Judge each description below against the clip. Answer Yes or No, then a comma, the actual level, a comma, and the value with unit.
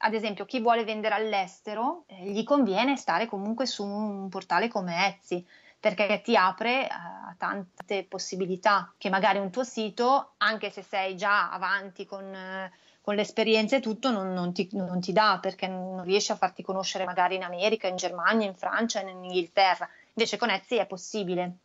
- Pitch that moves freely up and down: No, narrow, 2.5 semitones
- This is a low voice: No, high, 200 Hz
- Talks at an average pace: No, fast, 180 wpm